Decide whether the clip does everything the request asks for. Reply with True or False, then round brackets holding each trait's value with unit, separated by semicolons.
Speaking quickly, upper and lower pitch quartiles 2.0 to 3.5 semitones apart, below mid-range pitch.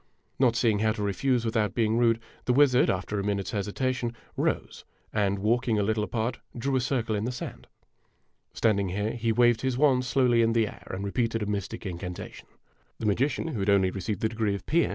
True (210 wpm; 3.1 semitones; 110 Hz)